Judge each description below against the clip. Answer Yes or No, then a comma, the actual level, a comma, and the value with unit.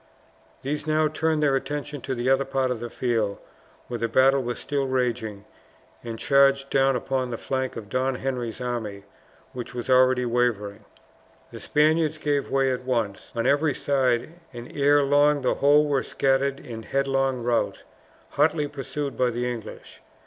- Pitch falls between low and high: No, low, 130 Hz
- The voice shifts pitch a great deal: No, average, 2.7 semitones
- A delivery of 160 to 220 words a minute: Yes, average, 165 wpm